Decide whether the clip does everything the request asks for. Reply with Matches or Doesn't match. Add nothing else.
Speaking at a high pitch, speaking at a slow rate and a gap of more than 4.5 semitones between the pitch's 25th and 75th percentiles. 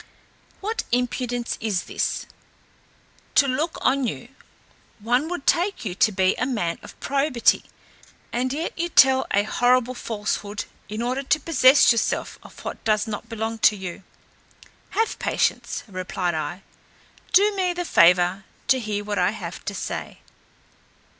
Doesn't match